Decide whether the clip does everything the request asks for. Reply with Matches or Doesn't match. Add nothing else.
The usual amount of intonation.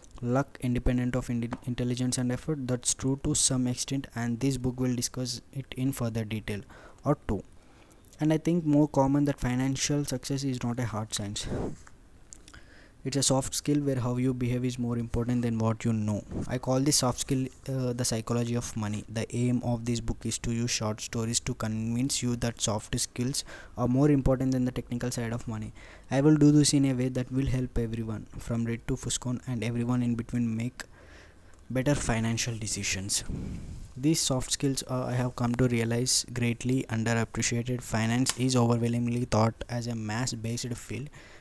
Doesn't match